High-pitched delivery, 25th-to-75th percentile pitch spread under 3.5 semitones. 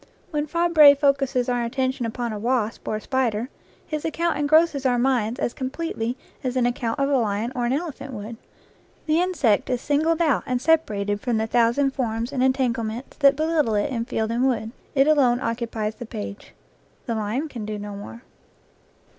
No: very high, 250 Hz; average, 3.8 semitones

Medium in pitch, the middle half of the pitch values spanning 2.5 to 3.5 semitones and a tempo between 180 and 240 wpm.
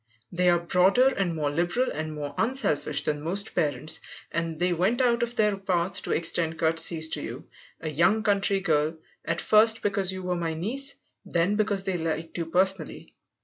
No: medium, 175 Hz; average, 3.9 semitones; average, 185 wpm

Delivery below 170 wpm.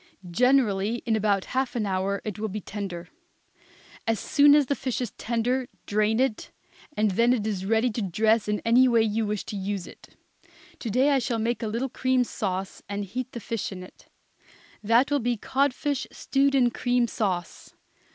No: average, 190 wpm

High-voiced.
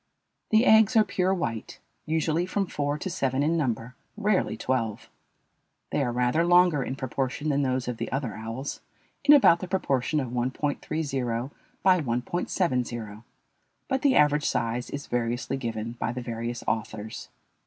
No: low, 135 Hz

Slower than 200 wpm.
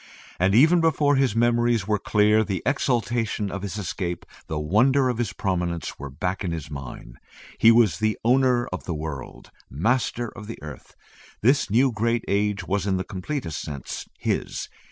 Yes: average, 170 wpm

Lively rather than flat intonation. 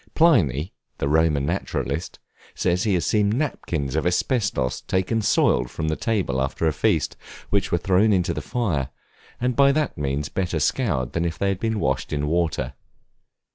Yes: wide, 6.2 semitones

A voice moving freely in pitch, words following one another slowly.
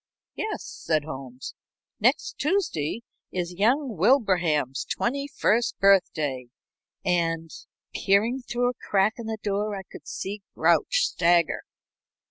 Yes: wide, 6.4 semitones; slow, 120 wpm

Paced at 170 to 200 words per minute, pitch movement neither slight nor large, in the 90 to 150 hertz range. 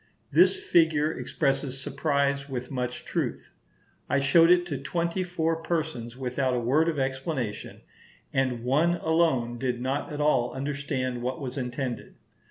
No: average, 145 wpm; average, 4.0 semitones; medium, 140 Hz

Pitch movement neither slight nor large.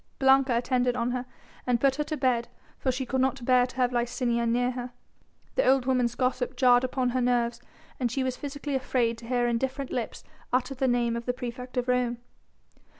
No: narrow, 1.3 semitones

